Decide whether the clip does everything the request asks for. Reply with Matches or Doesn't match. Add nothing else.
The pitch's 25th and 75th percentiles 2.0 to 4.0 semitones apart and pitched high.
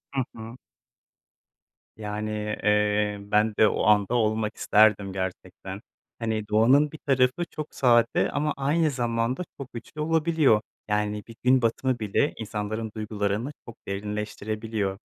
Doesn't match